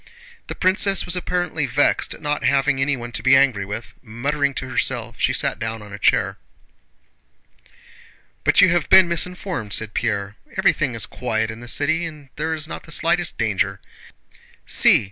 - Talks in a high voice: No, medium, 140 Hz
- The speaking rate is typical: Yes, average, 170 wpm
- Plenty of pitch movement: Yes, wide, 6.4 semitones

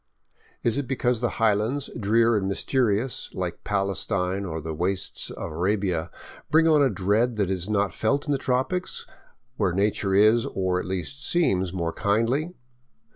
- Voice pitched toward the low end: Yes, low, 105 Hz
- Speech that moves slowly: No, average, 160 wpm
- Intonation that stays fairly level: No, average, 4.6 semitones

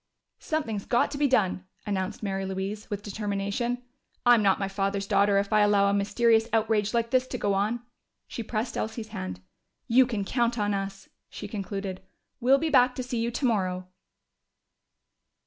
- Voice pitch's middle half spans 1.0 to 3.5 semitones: Yes, average, 3.2 semitones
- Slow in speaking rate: No, average, 170 wpm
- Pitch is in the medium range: No, high, 210 Hz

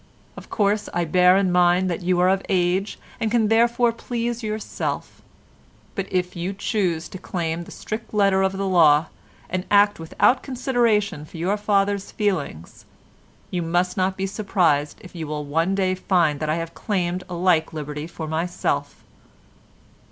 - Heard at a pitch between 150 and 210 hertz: Yes, medium, 185 Hz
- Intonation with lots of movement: No, average, 3.4 semitones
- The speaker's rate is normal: Yes, average, 165 wpm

